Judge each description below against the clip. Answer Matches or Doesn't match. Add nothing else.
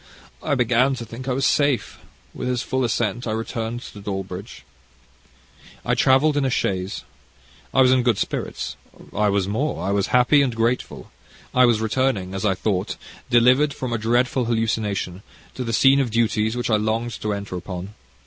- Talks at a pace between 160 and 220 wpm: Matches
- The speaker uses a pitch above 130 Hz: Doesn't match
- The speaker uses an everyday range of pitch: Matches